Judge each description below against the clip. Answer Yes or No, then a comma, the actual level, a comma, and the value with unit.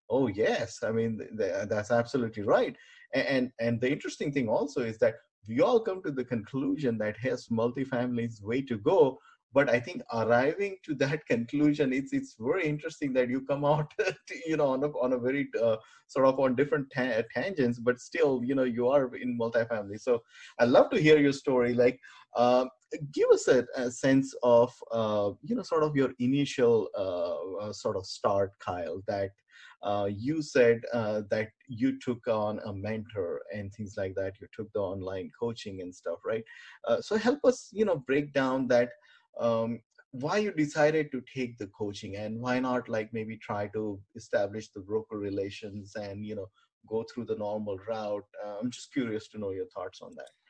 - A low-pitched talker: Yes, low, 125 Hz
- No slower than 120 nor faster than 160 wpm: No, average, 195 wpm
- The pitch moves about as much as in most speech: Yes, average, 4.5 semitones